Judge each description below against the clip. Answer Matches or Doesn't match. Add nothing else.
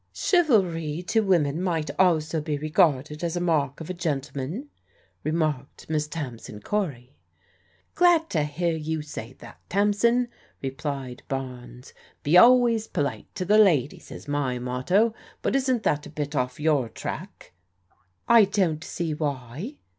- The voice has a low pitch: Doesn't match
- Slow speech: Doesn't match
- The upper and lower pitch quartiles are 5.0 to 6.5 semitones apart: Matches